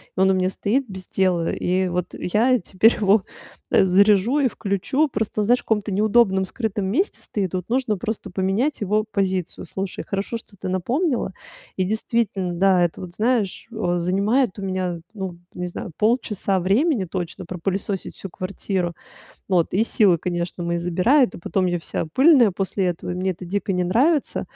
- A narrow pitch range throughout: No, average, 3.3 semitones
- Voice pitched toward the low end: No, high, 195 Hz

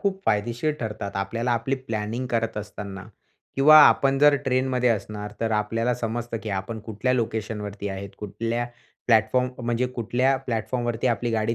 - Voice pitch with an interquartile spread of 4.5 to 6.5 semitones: No, average, 2.9 semitones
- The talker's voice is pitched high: No, low, 115 Hz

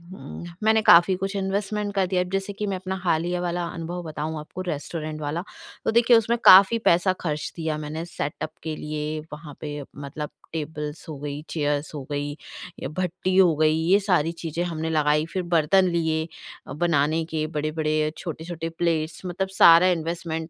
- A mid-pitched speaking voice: Yes, medium, 165 Hz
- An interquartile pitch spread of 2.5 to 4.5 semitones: Yes, average, 3.1 semitones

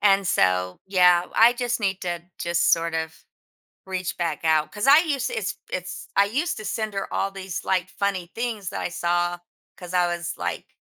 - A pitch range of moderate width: Yes, average, 3.2 semitones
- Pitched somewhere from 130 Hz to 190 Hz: Yes, medium, 185 Hz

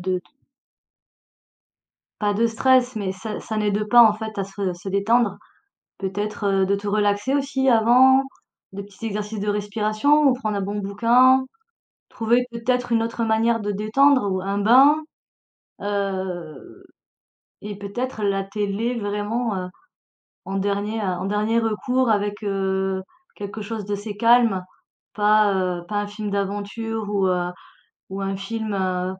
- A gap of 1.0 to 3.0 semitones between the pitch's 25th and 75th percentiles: Yes, narrow, 2.5 semitones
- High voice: Yes, high, 210 Hz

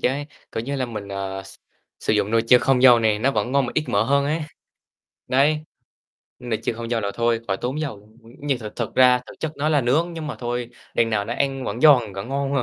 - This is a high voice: No, low, 125 Hz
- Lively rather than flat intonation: No, average, 3.8 semitones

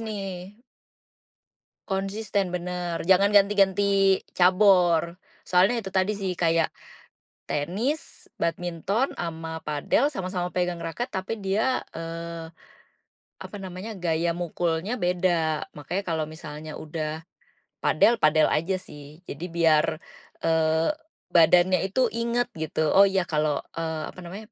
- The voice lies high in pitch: No, medium, 180 Hz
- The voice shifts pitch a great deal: No, average, 3.2 semitones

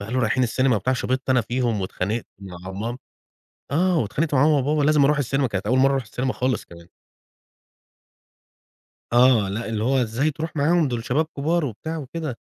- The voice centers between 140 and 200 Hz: No, low, 130 Hz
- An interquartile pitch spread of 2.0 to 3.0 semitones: No, average, 4.4 semitones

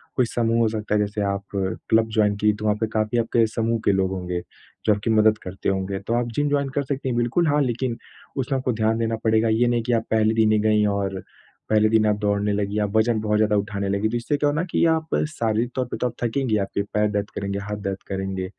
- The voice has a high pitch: No, low, 110 Hz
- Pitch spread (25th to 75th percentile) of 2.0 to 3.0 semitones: Yes, narrow, 2.4 semitones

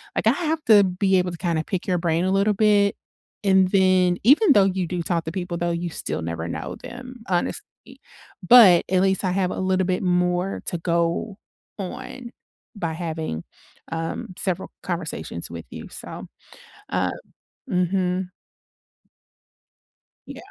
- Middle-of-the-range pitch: Yes, medium, 180 Hz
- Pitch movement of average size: No, narrow, 2.3 semitones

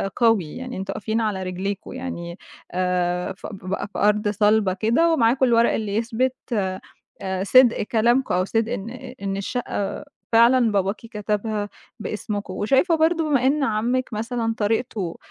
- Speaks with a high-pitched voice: Yes, high, 220 Hz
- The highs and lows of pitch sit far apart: No, average, 3.7 semitones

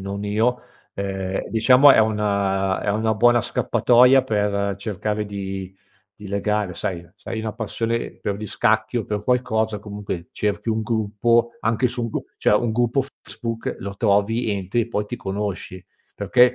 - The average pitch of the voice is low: Yes, low, 105 Hz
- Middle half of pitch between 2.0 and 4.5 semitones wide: Yes, narrow, 2.5 semitones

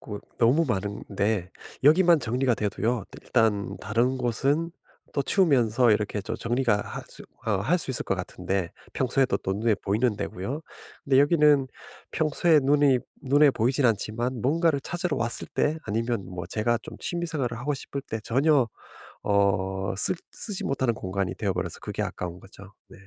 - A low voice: Yes, low, 120 Hz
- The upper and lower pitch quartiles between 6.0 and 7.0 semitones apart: No, wide, 5.5 semitones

